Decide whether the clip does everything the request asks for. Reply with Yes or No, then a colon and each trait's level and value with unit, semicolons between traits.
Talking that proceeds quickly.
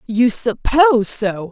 No: slow, 120 wpm